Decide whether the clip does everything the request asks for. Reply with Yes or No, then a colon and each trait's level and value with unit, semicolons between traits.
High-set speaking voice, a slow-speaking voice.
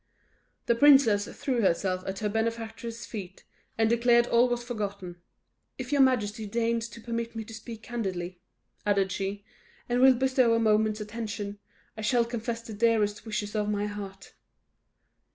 No: high, 225 Hz; average, 155 wpm